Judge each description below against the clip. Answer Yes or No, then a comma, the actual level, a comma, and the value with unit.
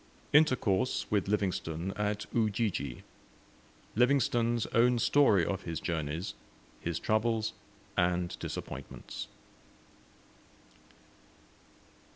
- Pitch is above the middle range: No, low, 105 Hz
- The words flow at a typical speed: No, slow, 75 wpm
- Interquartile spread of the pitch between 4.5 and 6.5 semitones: Yes, average, 4.9 semitones